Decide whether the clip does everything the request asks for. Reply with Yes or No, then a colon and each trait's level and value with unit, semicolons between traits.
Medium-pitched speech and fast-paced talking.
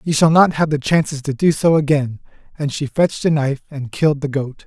Yes: medium, 145 Hz; fast, 245 wpm